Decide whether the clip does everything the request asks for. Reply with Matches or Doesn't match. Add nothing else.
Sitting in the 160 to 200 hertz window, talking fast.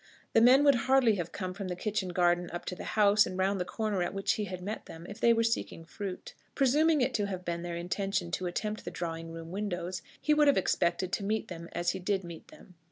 Matches